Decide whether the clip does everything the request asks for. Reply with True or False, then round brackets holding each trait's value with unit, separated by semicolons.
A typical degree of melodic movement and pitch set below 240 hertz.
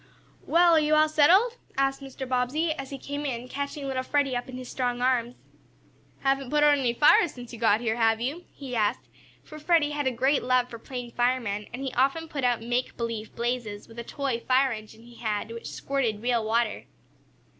False (3.2 semitones; 255 Hz)